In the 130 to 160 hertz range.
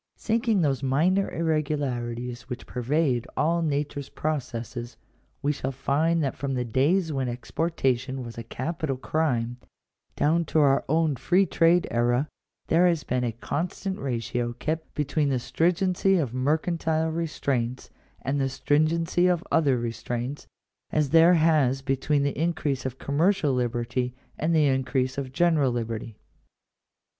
Yes: medium, 140 Hz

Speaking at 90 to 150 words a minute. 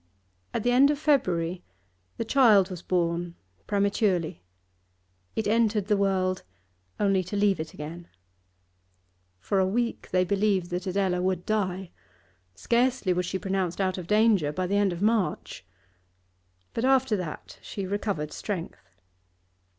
Yes: average, 140 wpm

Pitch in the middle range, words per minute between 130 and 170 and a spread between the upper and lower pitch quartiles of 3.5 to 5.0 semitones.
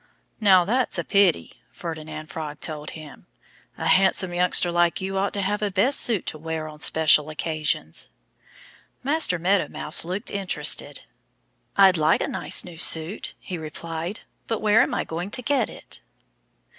Yes: medium, 175 Hz; average, 160 wpm; average, 4.0 semitones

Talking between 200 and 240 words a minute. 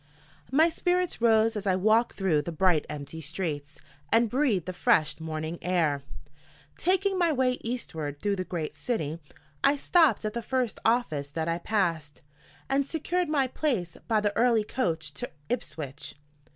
No: average, 160 wpm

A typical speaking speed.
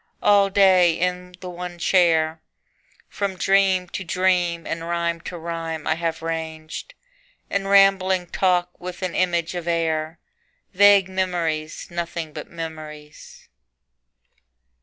No: slow, 120 wpm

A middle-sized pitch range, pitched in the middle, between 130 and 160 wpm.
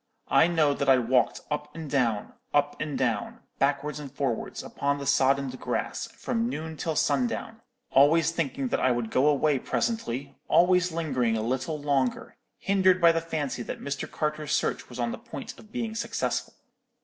No: average, 4.0 semitones; medium, 145 Hz; average, 175 wpm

